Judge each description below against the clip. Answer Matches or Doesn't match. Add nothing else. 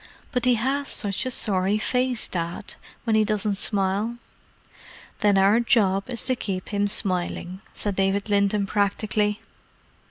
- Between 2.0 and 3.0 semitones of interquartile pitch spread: Matches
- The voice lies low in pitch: Doesn't match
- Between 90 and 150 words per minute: Matches